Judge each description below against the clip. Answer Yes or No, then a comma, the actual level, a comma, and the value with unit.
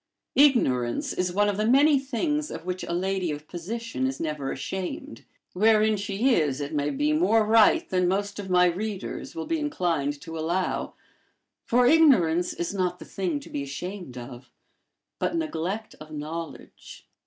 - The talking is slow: No, average, 165 wpm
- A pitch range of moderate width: No, wide, 6.0 semitones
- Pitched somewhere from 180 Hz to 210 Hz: Yes, medium, 185 Hz